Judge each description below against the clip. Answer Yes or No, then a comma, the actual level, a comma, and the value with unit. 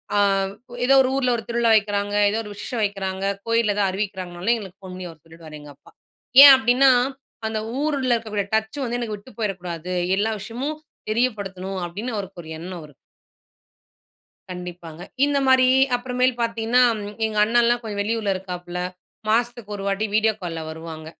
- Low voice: No, high, 210 Hz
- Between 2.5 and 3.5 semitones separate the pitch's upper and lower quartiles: No, average, 4.3 semitones